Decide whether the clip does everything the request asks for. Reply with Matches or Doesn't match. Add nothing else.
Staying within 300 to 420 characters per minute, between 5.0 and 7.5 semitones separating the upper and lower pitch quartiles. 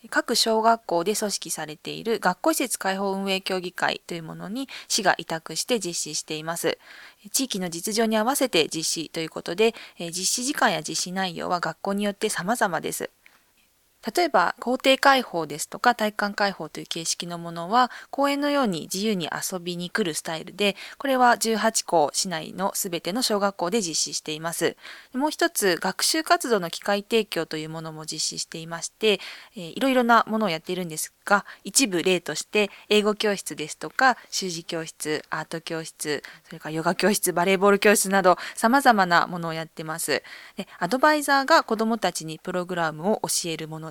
Matches